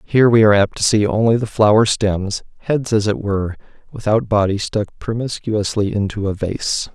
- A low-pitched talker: Yes, low, 105 Hz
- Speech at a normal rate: Yes, average, 180 wpm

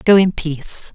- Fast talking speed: No, average, 190 wpm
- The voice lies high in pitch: No, medium, 170 Hz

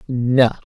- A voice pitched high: No, low, 125 Hz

